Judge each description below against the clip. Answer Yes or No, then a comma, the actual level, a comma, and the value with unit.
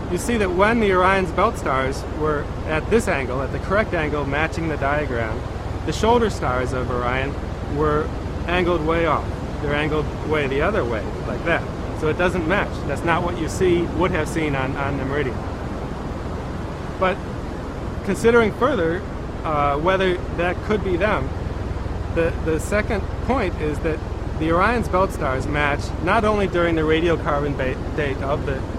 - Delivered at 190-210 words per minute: No, average, 165 wpm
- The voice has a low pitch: No, medium, 145 Hz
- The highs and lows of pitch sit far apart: Yes, wide, 7.2 semitones